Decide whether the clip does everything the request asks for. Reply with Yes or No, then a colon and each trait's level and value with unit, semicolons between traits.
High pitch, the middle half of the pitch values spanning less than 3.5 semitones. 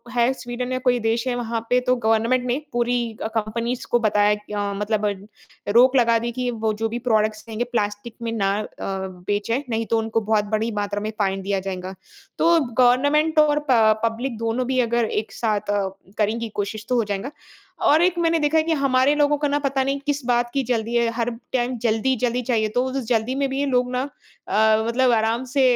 Yes: high, 235 Hz; average, 2.8 semitones